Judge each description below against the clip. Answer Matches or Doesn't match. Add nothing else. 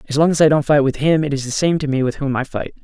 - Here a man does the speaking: Matches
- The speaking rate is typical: Doesn't match